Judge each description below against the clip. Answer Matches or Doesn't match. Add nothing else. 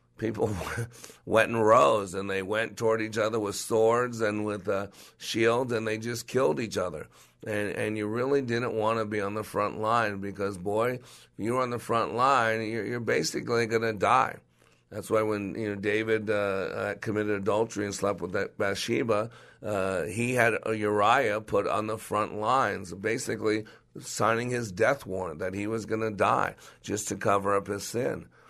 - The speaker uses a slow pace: Doesn't match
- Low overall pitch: Matches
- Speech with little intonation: Matches